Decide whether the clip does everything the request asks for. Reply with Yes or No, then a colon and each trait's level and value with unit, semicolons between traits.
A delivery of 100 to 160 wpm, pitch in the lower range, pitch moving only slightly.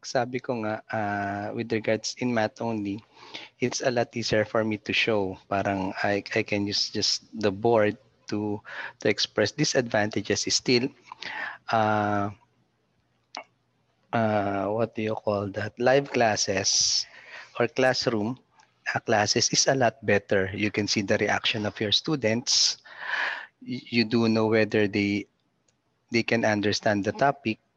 Yes: average, 140 wpm; low, 110 Hz; narrow, 2.3 semitones